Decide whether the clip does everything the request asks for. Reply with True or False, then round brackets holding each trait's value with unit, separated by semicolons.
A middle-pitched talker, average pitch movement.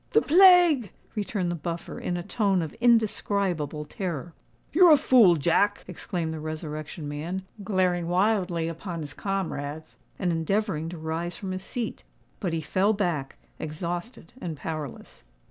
True (175 Hz; 4.0 semitones)